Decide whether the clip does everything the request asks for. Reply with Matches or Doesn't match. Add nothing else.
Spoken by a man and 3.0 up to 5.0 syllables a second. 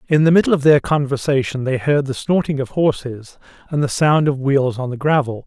Doesn't match